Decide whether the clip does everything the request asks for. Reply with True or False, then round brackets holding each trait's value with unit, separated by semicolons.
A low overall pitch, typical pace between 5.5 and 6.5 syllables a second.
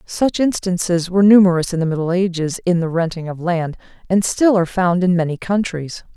False (180 Hz; 5.6 syllables/s)